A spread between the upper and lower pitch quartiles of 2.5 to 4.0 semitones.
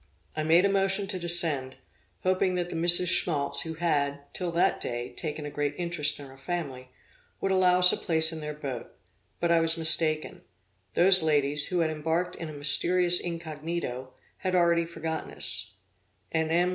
Yes: average, 2.9 semitones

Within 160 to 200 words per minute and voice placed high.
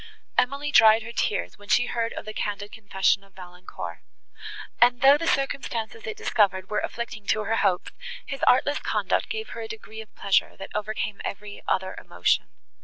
Yes: average, 180 wpm; high, 220 Hz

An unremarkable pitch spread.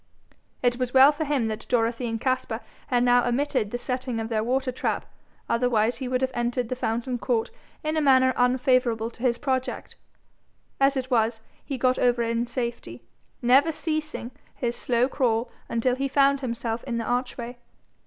No: narrow, 1.9 semitones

